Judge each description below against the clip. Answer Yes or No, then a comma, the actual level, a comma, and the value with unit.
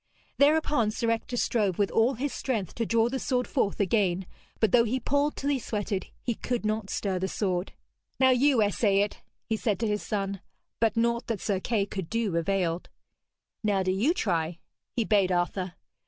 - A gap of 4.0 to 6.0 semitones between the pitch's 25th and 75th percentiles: No, average, 3.6 semitones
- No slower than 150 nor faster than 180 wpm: No, average, 190 wpm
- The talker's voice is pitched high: Yes, high, 215 Hz